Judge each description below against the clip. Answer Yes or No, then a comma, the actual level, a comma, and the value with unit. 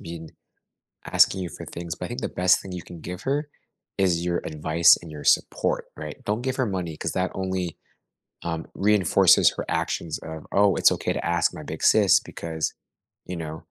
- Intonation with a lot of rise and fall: No, average, 2.9 semitones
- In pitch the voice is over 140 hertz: No, very low, 85 Hz